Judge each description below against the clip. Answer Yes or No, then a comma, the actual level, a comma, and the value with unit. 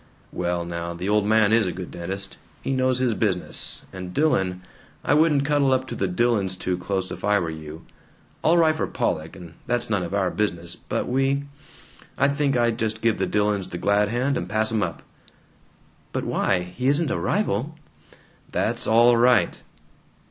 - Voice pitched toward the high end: No, low, 105 Hz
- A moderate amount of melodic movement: No, wide, 5.8 semitones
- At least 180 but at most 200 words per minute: Yes, average, 185 wpm